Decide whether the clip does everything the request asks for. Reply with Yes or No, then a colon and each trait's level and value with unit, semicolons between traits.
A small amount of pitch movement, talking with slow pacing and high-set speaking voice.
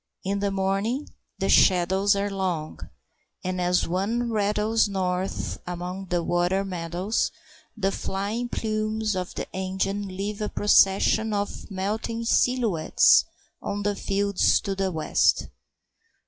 Yes: narrow, 2.2 semitones; slow, 125 wpm; high, 195 Hz